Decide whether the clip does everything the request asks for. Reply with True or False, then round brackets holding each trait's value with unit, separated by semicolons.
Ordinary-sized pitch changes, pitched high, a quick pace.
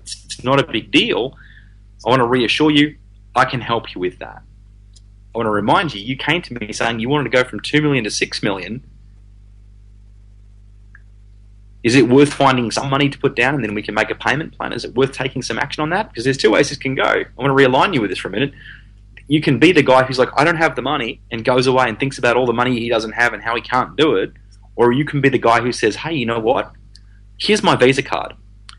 False (4.8 semitones; 115 Hz; 260 wpm)